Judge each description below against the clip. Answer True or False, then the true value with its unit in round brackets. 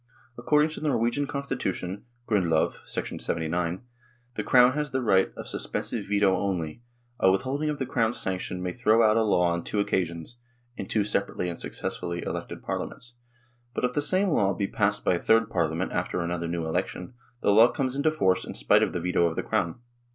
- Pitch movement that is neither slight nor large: False (5.8 semitones)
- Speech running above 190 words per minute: True (200 wpm)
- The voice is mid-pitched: False (100 Hz)